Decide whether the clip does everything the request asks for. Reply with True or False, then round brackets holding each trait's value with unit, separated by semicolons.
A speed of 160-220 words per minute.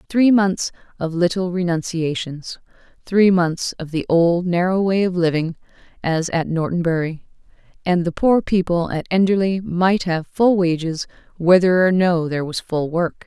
False (150 wpm)